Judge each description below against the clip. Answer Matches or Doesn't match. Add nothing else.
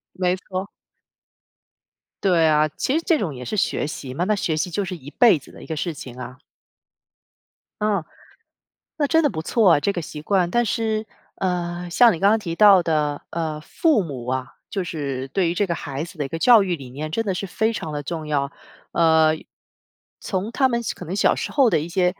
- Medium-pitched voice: Matches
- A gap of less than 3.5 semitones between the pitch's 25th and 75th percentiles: Doesn't match